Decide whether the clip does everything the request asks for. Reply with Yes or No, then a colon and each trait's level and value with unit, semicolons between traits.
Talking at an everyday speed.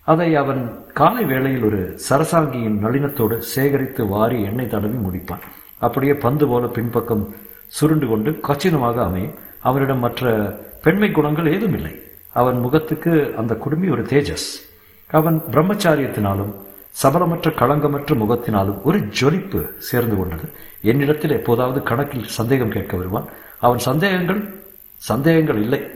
Yes: average, 120 wpm